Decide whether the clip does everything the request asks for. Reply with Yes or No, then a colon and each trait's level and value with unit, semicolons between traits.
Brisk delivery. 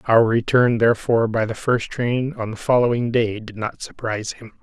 No: average, 195 wpm